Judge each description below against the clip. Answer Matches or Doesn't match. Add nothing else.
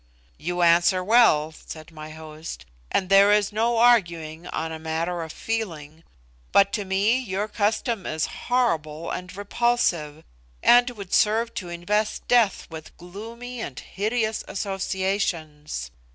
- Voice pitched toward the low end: Doesn't match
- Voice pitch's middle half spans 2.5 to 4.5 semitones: Doesn't match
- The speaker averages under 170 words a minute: Matches